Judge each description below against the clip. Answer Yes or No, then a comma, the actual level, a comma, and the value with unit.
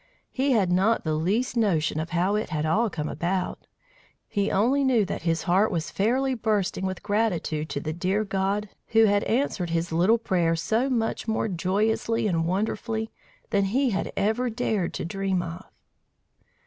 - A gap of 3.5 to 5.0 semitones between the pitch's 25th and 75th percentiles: Yes, average, 4.3 semitones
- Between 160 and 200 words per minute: Yes, average, 175 wpm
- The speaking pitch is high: Yes, high, 200 Hz